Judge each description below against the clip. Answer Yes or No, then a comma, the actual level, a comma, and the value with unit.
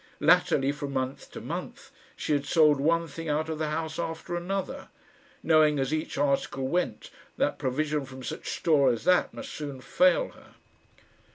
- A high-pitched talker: No, medium, 150 Hz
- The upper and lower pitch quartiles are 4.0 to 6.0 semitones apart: No, average, 2.8 semitones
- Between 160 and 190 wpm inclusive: Yes, average, 170 wpm